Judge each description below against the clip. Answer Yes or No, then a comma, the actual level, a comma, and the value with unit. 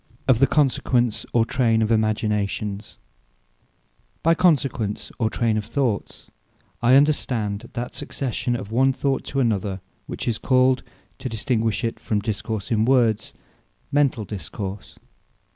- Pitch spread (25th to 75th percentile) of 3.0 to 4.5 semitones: Yes, average, 3.4 semitones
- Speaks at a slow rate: Yes, slow, 130 wpm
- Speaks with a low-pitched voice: Yes, low, 115 Hz